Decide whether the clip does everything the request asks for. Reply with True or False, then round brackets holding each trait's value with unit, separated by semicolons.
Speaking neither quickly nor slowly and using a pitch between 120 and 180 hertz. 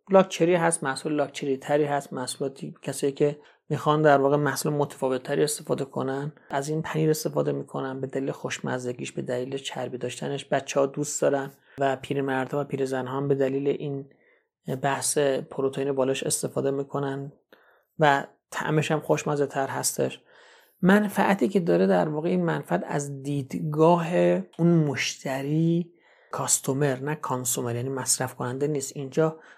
True (145 wpm; 140 Hz)